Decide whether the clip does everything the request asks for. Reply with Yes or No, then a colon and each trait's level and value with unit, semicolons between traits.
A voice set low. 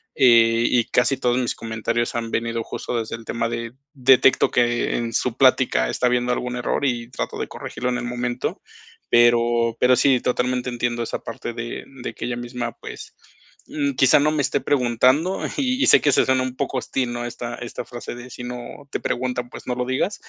Yes: low, 120 Hz